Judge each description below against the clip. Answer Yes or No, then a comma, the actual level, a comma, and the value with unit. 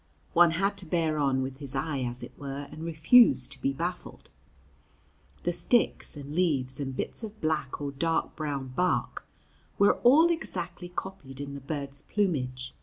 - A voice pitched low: No, medium, 150 Hz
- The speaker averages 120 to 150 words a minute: No, average, 170 wpm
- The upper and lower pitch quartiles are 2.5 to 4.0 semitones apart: No, average, 4.6 semitones